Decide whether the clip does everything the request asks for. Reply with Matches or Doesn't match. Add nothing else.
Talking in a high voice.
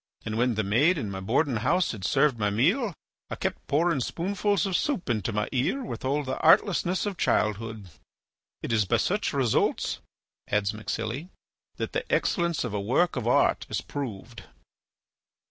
Doesn't match